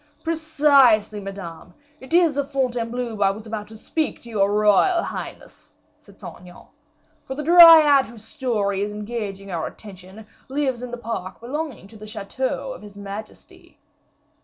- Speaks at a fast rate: No, average, 160 wpm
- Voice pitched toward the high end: Yes, high, 230 Hz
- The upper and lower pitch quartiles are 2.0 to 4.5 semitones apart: No, average, 5.2 semitones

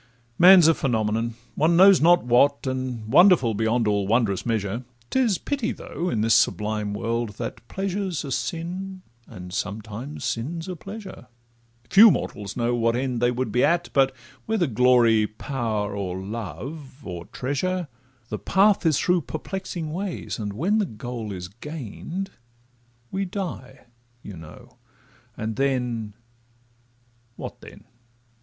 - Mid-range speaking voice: No, low, 125 Hz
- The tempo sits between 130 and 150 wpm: Yes, average, 145 wpm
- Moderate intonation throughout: No, wide, 7.9 semitones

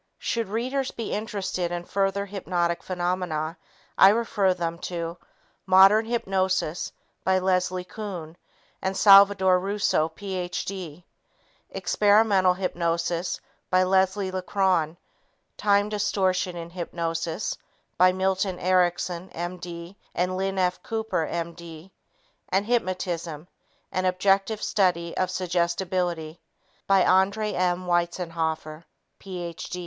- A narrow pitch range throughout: Yes, narrow, 2.1 semitones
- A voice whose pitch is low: No, medium, 185 Hz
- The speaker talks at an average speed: No, slow, 100 wpm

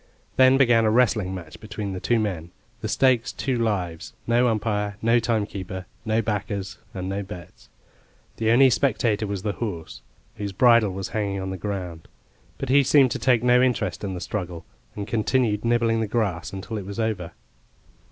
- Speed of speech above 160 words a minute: Yes, average, 180 wpm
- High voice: No, low, 105 Hz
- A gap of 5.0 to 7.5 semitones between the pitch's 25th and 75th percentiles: No, average, 3.5 semitones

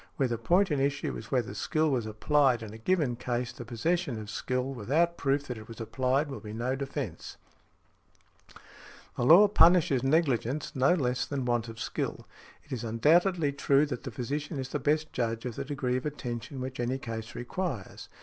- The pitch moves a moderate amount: Yes, average, 3.7 semitones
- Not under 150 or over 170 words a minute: No, average, 190 wpm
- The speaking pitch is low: Yes, low, 130 Hz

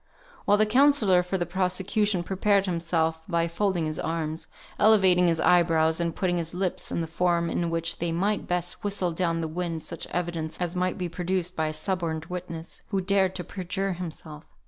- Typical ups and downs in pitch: No, narrow, 2.2 semitones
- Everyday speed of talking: Yes, average, 190 wpm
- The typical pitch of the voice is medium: Yes, medium, 175 Hz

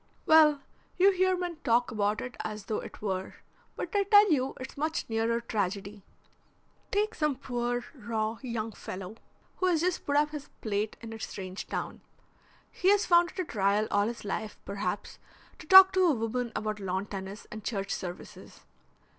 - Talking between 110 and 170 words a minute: No, average, 180 wpm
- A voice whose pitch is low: No, high, 235 Hz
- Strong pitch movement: Yes, wide, 7.2 semitones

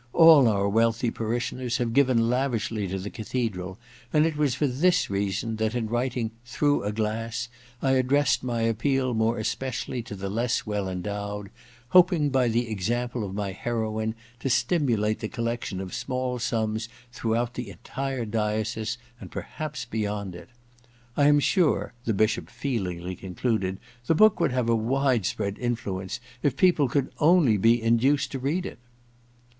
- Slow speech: No, average, 160 wpm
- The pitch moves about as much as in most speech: Yes, average, 3.5 semitones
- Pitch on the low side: Yes, low, 115 Hz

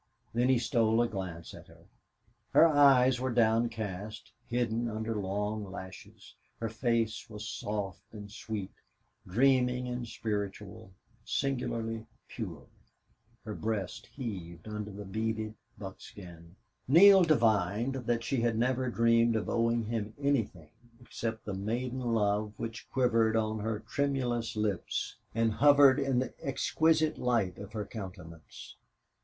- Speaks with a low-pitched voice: Yes, low, 110 Hz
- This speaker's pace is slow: Yes, slow, 125 wpm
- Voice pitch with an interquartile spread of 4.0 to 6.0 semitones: No, average, 3.1 semitones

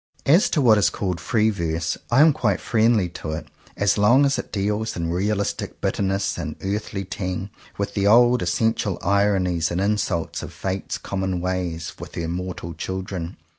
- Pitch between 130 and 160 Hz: No, low, 100 Hz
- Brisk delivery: No, average, 175 wpm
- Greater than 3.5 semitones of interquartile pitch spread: No, average, 3.1 semitones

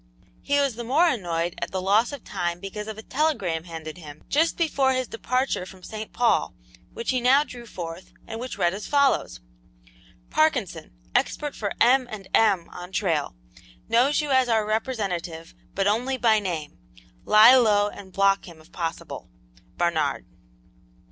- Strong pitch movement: Yes, wide, 6.2 semitones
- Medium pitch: No, high, 215 Hz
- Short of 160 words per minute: No, average, 165 wpm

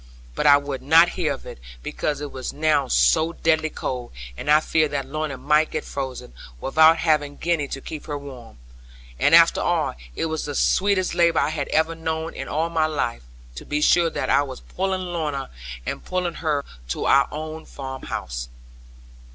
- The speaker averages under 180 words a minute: No, average, 185 wpm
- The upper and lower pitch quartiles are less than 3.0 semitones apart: Yes, narrow, 2.6 semitones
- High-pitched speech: No, medium, 155 Hz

